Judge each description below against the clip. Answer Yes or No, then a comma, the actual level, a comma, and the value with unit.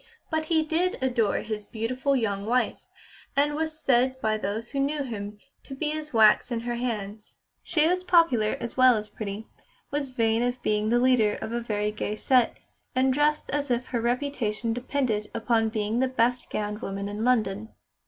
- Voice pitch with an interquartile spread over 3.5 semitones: Yes, average, 4.0 semitones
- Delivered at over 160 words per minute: Yes, average, 185 wpm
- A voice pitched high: Yes, high, 240 Hz